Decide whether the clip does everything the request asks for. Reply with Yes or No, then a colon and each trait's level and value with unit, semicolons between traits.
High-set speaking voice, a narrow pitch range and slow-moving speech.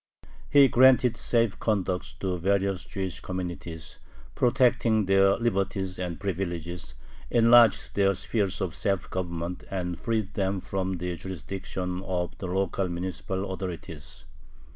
No: very low, 95 Hz; narrow, 2.1 semitones; slow, 120 wpm